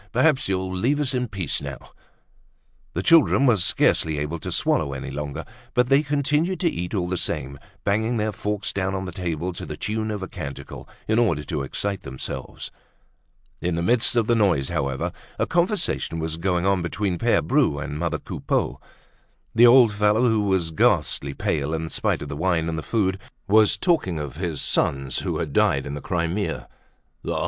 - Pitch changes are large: Yes, wide, 5.9 semitones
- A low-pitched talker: Yes, very low, 95 Hz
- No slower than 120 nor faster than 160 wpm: No, average, 190 wpm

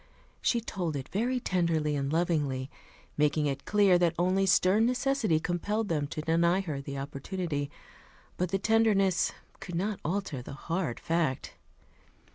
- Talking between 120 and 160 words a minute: Yes, average, 145 wpm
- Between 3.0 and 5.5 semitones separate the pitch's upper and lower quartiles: Yes, average, 4.7 semitones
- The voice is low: No, medium, 170 Hz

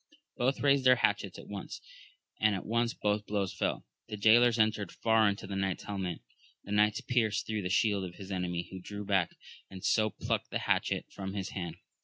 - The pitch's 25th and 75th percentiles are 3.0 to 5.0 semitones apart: No, narrow, 2.4 semitones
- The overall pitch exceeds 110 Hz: No, low, 105 Hz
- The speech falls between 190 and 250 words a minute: Yes, average, 200 wpm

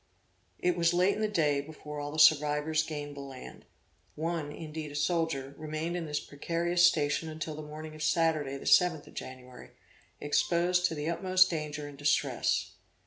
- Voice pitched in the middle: Yes, medium, 155 Hz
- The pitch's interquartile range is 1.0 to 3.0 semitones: Yes, narrow, 2.4 semitones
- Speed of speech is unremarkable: Yes, average, 175 wpm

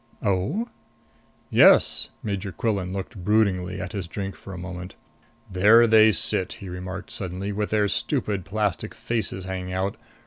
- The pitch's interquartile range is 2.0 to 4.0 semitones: Yes, narrow, 2.4 semitones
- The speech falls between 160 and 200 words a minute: No, average, 145 wpm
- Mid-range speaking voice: No, very low, 95 Hz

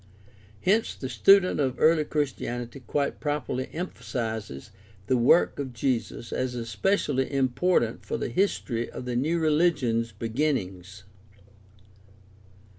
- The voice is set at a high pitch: No, low, 130 Hz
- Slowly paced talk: Yes, slow, 115 wpm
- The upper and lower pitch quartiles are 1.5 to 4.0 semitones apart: No, average, 4.7 semitones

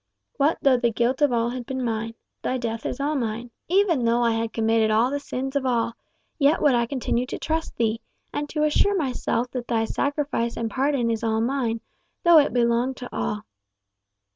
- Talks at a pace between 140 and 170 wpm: No, average, 200 wpm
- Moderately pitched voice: No, high, 245 Hz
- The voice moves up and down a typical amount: Yes, average, 3.4 semitones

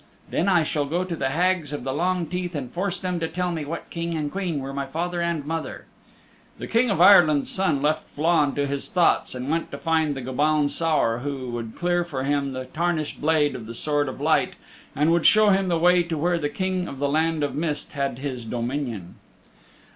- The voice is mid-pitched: Yes, medium, 155 Hz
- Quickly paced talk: Yes, fast, 220 wpm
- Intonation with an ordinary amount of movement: Yes, average, 3.7 semitones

